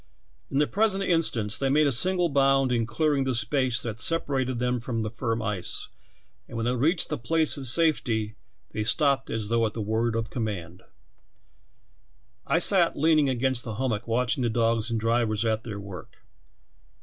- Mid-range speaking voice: No, low, 120 Hz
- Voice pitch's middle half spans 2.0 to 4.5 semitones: Yes, average, 3.9 semitones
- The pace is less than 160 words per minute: No, average, 180 wpm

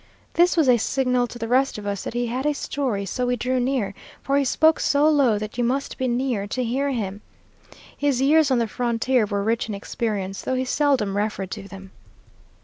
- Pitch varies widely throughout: No, average, 4.2 semitones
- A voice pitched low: No, high, 245 Hz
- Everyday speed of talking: No, fast, 220 wpm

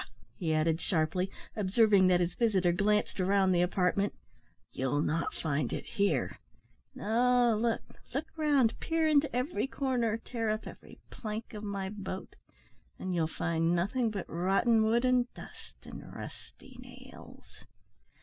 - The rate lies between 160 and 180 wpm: No, average, 140 wpm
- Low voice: No, high, 210 Hz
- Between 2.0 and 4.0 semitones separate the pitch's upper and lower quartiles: No, average, 5.1 semitones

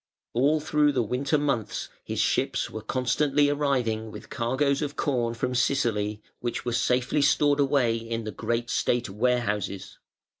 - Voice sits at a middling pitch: No, low, 125 Hz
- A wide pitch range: No, average, 3.6 semitones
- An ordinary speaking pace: Yes, average, 150 wpm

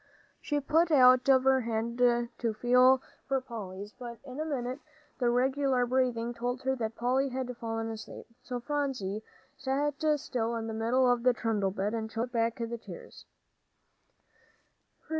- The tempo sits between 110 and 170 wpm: Yes, average, 160 wpm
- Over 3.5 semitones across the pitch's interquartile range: No, narrow, 2.4 semitones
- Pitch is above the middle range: Yes, high, 245 Hz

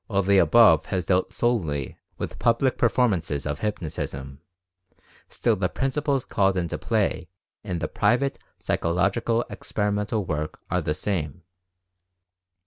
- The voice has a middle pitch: No, very low, 95 Hz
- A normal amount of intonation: No, wide, 5.8 semitones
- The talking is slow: Yes, slow, 130 wpm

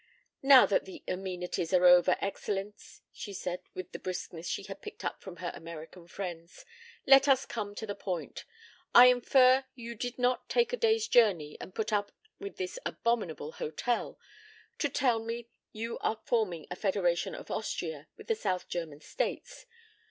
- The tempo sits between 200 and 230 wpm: No, average, 175 wpm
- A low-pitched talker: No, high, 200 Hz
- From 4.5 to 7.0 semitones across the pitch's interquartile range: Yes, wide, 5.5 semitones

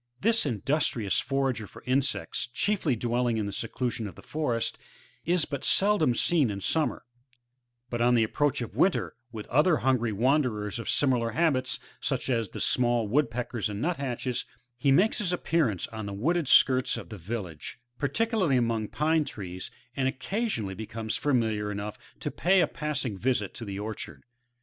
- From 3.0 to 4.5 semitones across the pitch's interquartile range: No, average, 5.2 semitones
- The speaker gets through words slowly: No, average, 165 wpm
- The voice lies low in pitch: Yes, low, 125 Hz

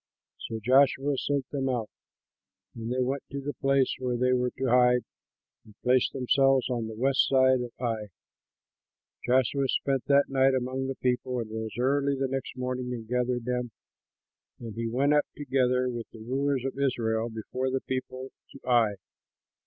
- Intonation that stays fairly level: Yes, narrow, 1.8 semitones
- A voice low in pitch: Yes, low, 130 Hz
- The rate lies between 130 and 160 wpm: No, average, 170 wpm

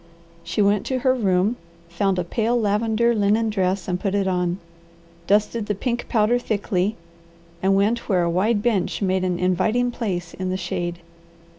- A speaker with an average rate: Yes, average, 170 wpm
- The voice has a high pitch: Yes, high, 200 Hz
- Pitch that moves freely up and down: No, average, 3.4 semitones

